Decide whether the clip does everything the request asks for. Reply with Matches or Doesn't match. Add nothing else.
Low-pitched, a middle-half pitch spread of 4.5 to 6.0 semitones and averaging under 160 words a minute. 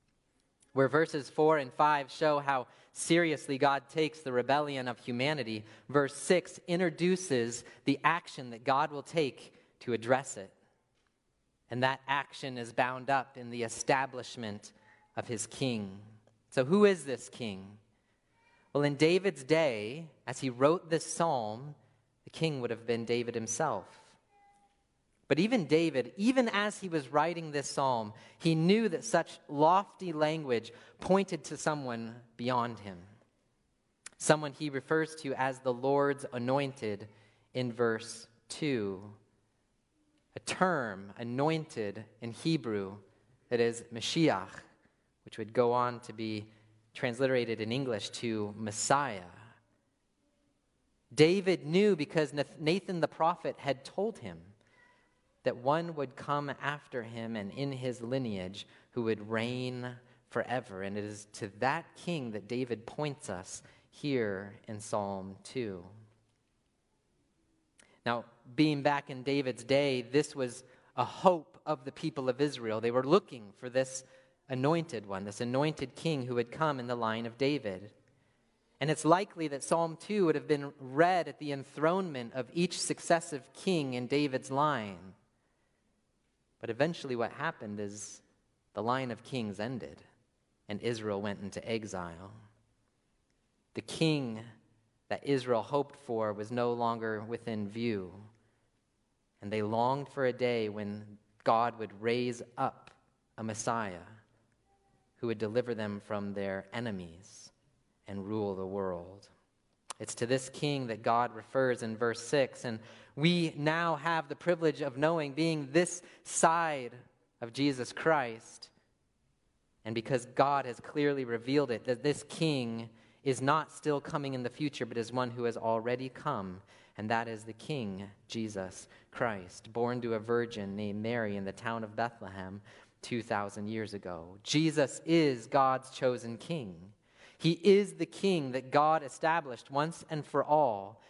Matches